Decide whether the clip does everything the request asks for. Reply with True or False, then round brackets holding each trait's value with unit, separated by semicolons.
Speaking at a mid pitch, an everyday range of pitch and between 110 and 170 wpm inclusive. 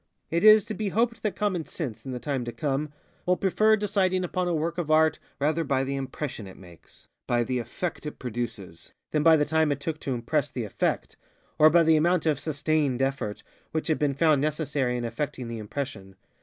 False (150 Hz; 4.5 semitones; 205 wpm)